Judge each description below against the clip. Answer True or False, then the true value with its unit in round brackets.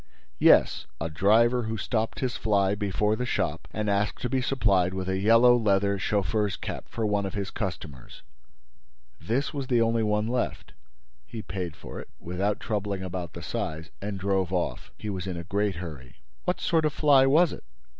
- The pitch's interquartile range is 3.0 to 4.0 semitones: True (3.5 semitones)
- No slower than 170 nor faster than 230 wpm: True (185 wpm)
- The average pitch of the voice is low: True (105 Hz)